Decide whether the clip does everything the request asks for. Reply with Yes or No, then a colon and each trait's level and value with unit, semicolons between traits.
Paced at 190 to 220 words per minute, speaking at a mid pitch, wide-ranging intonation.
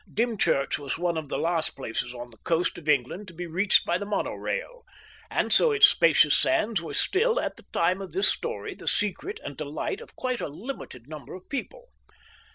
Yes: fast, 205 wpm; medium, 180 Hz; wide, 8.8 semitones